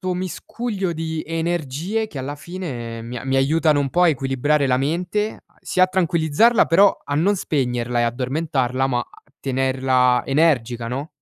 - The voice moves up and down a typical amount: Yes, average, 5.0 semitones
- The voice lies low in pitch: No, medium, 145 Hz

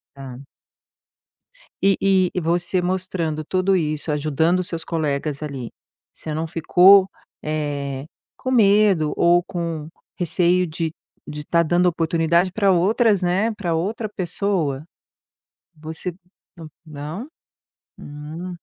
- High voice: No, medium, 170 Hz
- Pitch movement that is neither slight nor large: Yes, average, 3.2 semitones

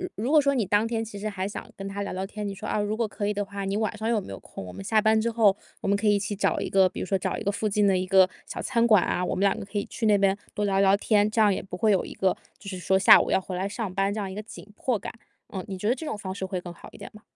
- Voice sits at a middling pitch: No, high, 200 Hz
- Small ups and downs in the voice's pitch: Yes, narrow, 2.0 semitones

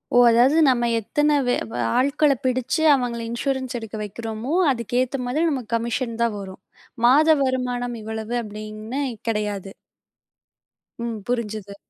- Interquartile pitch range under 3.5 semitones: Yes, average, 2.9 semitones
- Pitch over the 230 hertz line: Yes, high, 240 Hz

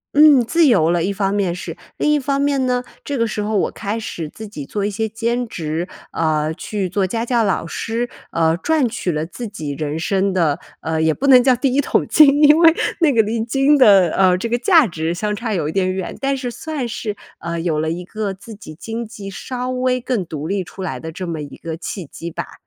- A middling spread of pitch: No, wide, 6.4 semitones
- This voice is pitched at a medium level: No, high, 205 Hz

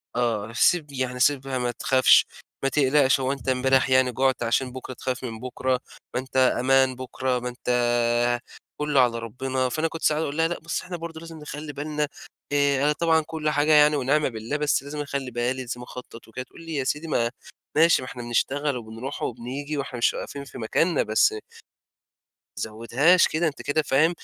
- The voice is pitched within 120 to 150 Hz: Yes, low, 135 Hz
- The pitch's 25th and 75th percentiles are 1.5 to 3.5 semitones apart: Yes, average, 3.0 semitones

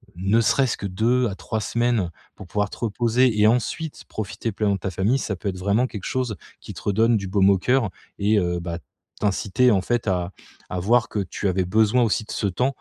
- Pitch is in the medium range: No, low, 105 Hz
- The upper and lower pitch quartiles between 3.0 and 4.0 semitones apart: Yes, average, 3.7 semitones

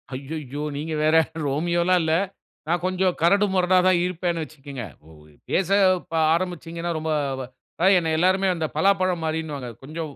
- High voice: No, medium, 165 Hz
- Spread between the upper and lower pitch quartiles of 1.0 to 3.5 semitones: Yes, average, 2.8 semitones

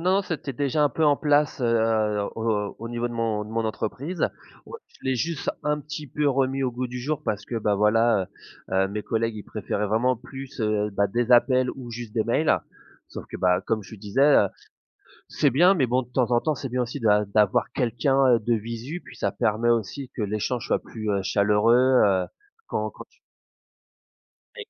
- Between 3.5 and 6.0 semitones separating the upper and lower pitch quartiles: Yes, average, 3.8 semitones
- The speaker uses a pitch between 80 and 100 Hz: No, low, 120 Hz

